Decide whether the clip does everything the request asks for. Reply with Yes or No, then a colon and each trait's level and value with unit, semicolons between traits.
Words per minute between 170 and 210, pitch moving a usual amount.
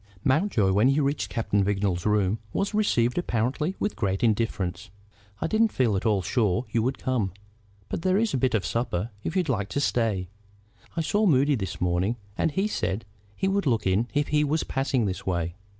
No: average, 195 wpm; wide, 6.8 semitones